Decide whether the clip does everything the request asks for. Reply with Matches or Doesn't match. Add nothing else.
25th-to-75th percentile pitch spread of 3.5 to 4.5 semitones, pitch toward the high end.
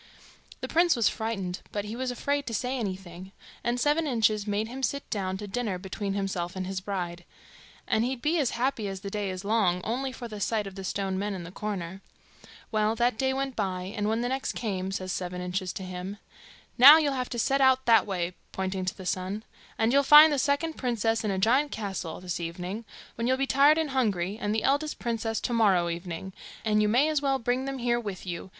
Doesn't match